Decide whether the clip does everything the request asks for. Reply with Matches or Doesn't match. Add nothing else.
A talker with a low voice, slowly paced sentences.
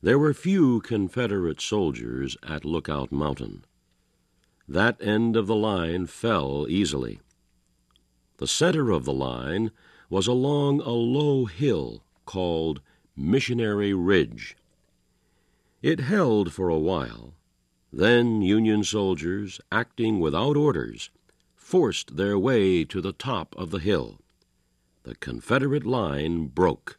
Matches